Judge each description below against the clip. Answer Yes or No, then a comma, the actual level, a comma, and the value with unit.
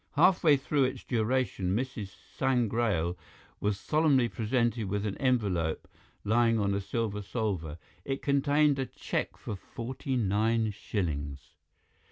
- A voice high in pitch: No, low, 115 Hz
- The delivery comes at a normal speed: No, slow, 125 wpm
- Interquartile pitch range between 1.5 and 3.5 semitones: No, average, 4.7 semitones